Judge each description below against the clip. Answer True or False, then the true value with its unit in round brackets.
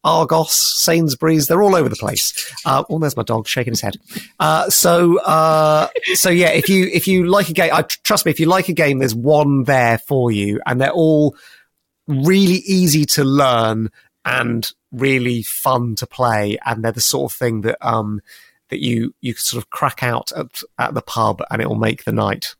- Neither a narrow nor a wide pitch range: False (5.9 semitones)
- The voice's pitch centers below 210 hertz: True (140 Hz)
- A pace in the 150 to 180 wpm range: False (200 wpm)